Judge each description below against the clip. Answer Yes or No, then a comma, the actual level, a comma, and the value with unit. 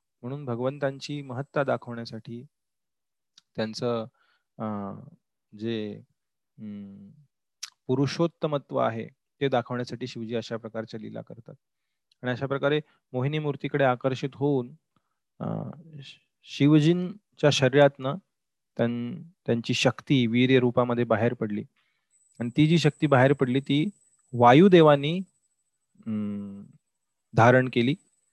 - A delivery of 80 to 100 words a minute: Yes, average, 85 wpm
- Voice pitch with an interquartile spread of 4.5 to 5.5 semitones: No, average, 3.8 semitones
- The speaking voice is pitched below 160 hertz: Yes, low, 135 Hz